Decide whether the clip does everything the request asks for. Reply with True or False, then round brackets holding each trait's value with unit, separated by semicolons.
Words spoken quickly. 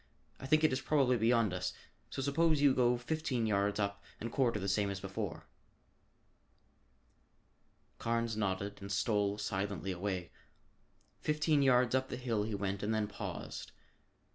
False (150 wpm)